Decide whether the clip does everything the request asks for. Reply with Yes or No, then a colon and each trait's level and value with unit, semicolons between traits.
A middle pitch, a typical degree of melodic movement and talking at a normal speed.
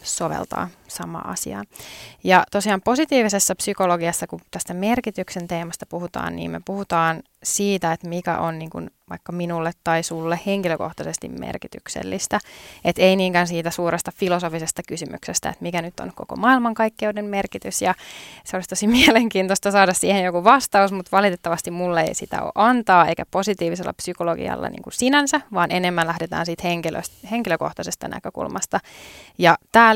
Yes: medium, 180 Hz; average, 3.0 semitones; average, 145 wpm